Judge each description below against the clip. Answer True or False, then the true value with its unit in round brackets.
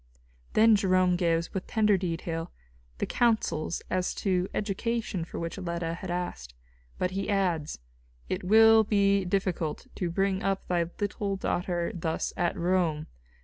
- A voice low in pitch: False (185 Hz)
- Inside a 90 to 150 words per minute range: True (145 wpm)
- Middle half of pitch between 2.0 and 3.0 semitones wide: True (2.6 semitones)